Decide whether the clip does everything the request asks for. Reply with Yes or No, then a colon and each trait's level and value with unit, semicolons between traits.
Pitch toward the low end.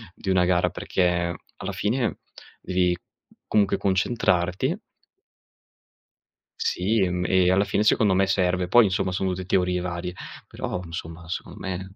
Yes: very low, 90 Hz